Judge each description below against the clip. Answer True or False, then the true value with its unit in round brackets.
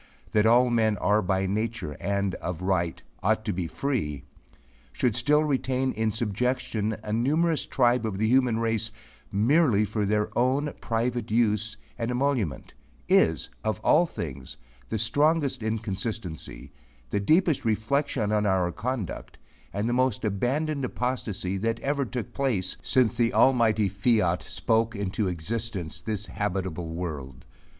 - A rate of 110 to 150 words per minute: True (140 wpm)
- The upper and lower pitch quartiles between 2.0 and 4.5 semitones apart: True (4.0 semitones)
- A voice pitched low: True (110 Hz)